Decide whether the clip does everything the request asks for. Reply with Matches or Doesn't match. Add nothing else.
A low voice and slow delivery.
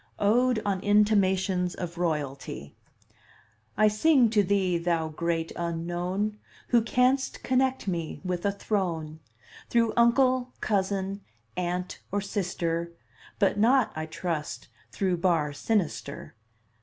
Doesn't match